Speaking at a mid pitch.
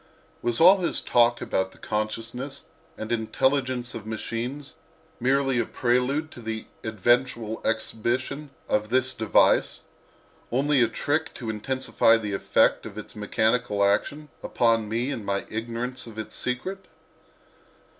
No: low, 120 Hz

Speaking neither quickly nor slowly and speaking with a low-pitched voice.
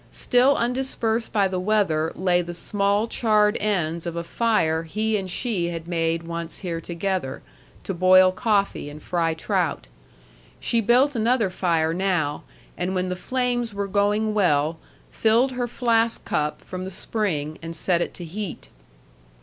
No: average, 160 wpm; high, 190 Hz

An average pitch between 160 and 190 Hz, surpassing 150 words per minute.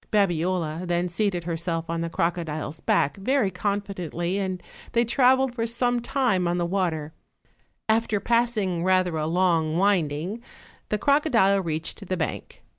No: medium, 185 Hz; average, 140 wpm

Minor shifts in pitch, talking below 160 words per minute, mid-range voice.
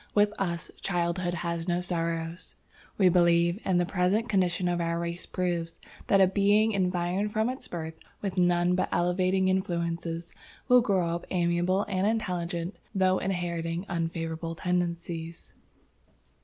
Yes: narrow, 1.9 semitones; average, 140 wpm; medium, 175 Hz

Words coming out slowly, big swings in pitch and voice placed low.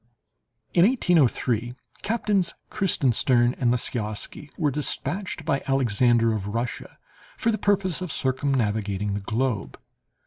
Yes: slow, 110 wpm; wide, 7.4 semitones; low, 130 Hz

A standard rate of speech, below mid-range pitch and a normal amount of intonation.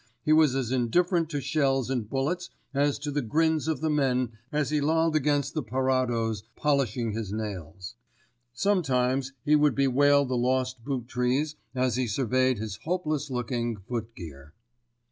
Yes: average, 160 wpm; low, 130 Hz; average, 3.9 semitones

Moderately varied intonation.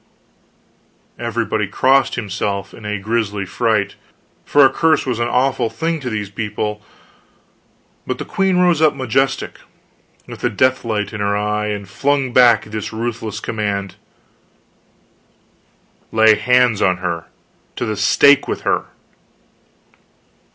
Yes: average, 3.9 semitones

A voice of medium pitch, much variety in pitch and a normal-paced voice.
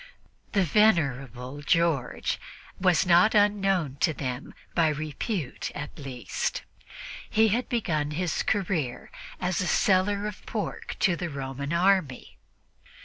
No: medium, 170 Hz; wide, 5.7 semitones; slow, 115 wpm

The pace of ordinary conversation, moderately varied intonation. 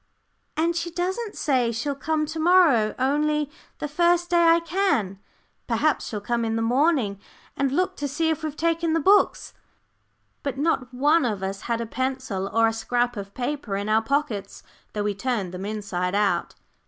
No: average, 180 wpm; wide, 6.7 semitones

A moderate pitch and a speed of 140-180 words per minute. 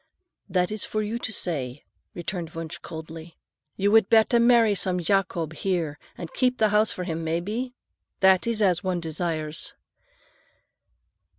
Yes: medium, 180 Hz; average, 155 wpm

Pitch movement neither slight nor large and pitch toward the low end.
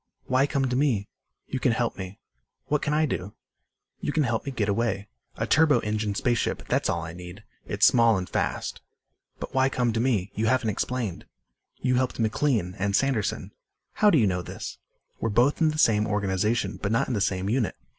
Yes: average, 4.5 semitones; low, 115 Hz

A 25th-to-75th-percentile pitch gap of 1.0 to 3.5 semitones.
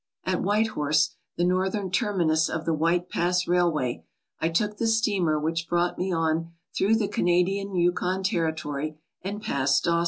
Yes: average, 3.2 semitones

